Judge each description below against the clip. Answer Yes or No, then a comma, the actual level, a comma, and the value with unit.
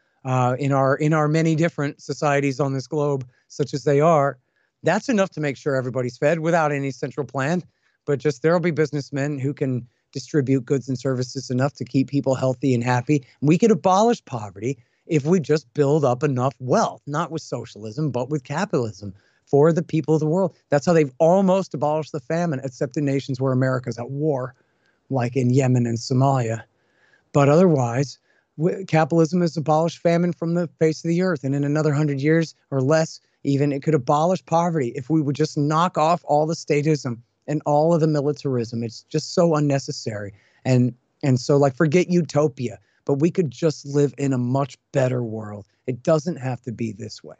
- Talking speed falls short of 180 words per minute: No, average, 190 wpm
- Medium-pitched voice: Yes, medium, 145 Hz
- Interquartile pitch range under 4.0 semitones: Yes, average, 3.3 semitones